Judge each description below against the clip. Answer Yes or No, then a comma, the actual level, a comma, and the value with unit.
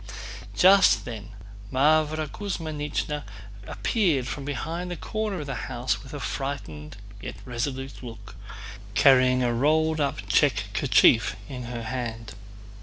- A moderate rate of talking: No, slow, 125 wpm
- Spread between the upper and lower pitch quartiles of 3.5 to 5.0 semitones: Yes, average, 4.4 semitones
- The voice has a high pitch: No, low, 135 Hz